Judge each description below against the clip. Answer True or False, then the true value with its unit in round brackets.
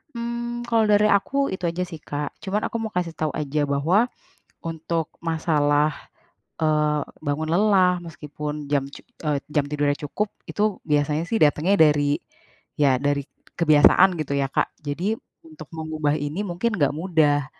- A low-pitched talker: False (155 Hz)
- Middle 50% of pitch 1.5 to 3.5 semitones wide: False (4.4 semitones)